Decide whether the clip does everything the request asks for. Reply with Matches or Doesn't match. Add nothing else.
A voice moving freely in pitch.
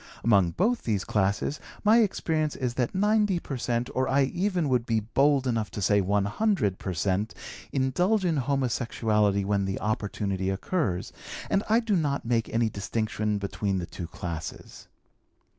Matches